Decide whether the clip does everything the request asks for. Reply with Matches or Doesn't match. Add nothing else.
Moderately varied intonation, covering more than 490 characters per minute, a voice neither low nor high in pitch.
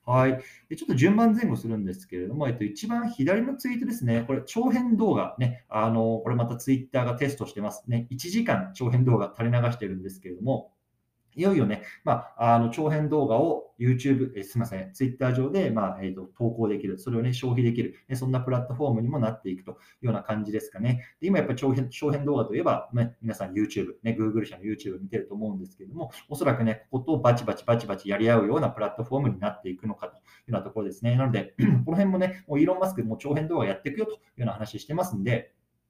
Doesn't match